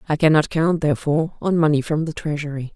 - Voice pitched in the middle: Yes, medium, 155 Hz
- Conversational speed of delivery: Yes, average, 195 wpm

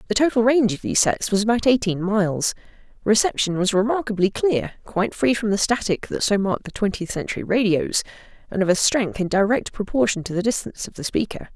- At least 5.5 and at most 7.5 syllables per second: Yes, 6.2 syllables/s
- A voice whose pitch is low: No, high, 210 Hz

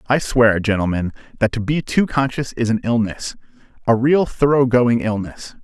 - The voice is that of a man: Yes, male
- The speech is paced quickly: No, average, 160 wpm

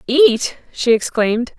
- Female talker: Yes, female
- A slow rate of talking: Yes, slow, 115 wpm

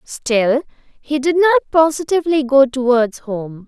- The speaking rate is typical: No, slow, 130 wpm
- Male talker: No, female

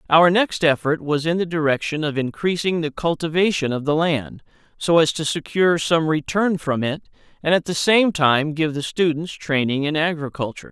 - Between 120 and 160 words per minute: No, average, 185 wpm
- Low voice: No, medium, 160 Hz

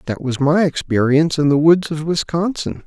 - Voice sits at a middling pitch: Yes, medium, 155 Hz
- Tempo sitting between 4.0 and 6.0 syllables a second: Yes, 5.2 syllables/s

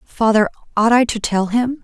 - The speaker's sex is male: No, female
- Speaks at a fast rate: No, average, 195 wpm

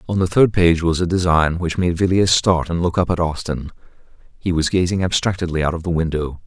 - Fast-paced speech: Yes, fast, 225 wpm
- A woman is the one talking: No, male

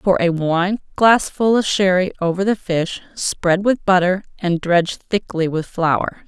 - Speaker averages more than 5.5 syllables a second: No, 4.1 syllables/s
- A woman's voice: Yes, female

